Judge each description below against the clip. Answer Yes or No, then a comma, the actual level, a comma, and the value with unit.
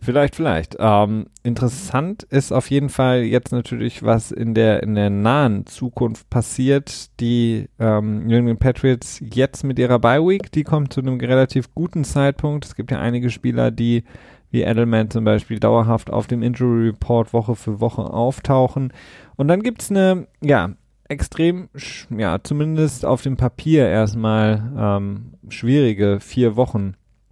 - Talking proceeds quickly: No, average, 155 wpm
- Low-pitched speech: Yes, low, 120 Hz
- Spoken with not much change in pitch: No, average, 3.4 semitones